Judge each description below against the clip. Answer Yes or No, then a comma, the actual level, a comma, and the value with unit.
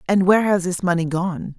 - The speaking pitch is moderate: Yes, medium, 180 Hz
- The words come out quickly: Yes, fast, 225 wpm